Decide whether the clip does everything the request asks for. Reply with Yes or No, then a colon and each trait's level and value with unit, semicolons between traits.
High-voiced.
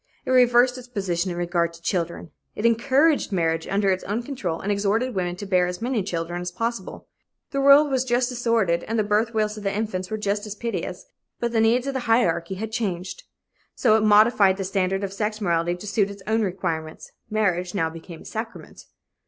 Yes: high, 205 Hz